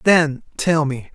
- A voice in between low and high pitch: Yes, medium, 150 Hz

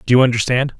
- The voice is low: Yes, low, 125 Hz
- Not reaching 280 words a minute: Yes, fast, 225 wpm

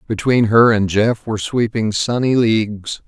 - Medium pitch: No, low, 110 Hz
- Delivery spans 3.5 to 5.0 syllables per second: Yes, 4.5 syllables/s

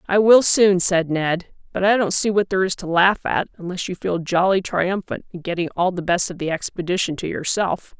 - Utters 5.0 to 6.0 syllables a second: Yes, 5.2 syllables/s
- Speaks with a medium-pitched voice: Yes, medium, 180 Hz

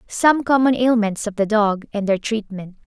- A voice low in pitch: No, high, 220 Hz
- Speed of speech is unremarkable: Yes, average, 190 wpm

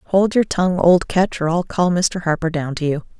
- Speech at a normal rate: No, fast, 245 wpm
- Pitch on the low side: No, medium, 170 Hz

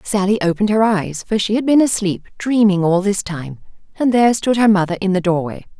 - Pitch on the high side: Yes, high, 200 Hz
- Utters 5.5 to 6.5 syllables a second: Yes, 5.8 syllables/s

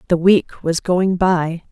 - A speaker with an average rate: Yes, average, 175 wpm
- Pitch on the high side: No, medium, 175 Hz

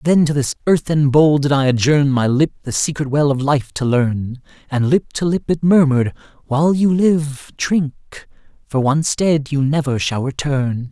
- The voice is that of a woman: No, male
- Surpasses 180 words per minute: No, average, 175 wpm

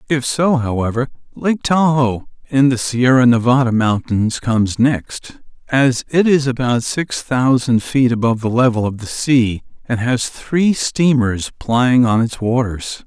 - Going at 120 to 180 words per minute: Yes, average, 150 wpm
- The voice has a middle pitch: No, low, 125 Hz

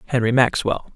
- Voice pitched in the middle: No, low, 120 Hz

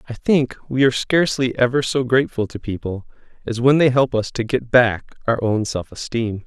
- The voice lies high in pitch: No, low, 120 Hz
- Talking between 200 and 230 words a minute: Yes, fast, 205 wpm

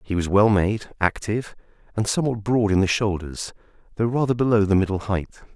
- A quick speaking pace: No, average, 185 wpm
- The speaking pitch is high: No, low, 105 Hz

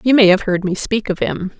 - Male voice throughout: No, female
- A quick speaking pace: Yes, fast, 300 wpm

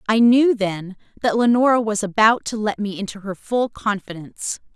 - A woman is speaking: Yes, female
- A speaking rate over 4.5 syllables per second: Yes, 5.0 syllables/s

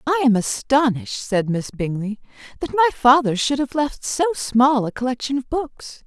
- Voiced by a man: No, female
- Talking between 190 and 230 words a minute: No, average, 180 wpm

